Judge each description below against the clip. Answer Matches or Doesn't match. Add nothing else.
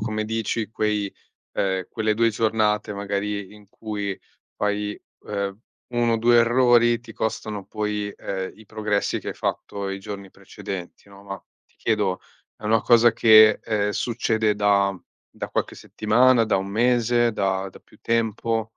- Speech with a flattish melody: Matches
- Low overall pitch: Matches